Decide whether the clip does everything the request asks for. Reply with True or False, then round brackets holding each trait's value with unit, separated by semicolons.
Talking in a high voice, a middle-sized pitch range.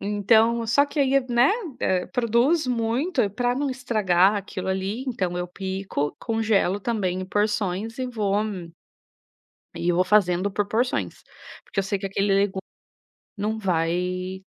True (205 Hz; 3.7 semitones)